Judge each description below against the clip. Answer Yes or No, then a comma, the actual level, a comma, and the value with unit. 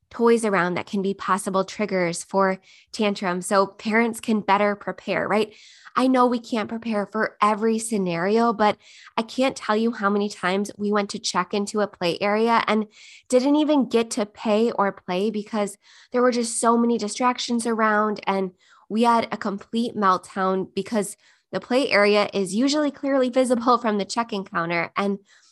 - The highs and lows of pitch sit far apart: No, average, 2.9 semitones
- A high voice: Yes, high, 210 Hz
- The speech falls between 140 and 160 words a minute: No, average, 175 wpm